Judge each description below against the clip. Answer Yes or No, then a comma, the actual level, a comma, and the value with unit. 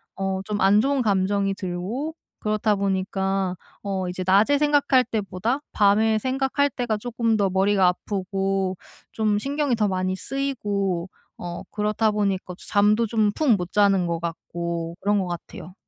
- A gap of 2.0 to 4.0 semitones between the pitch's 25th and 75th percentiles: Yes, average, 2.9 semitones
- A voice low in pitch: No, high, 200 Hz